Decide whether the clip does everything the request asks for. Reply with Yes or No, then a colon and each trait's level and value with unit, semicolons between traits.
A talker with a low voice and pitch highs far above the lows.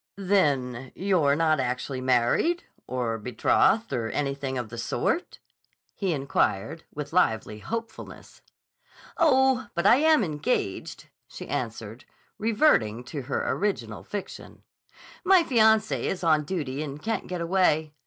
No: medium, 150 Hz; wide, 8.5 semitones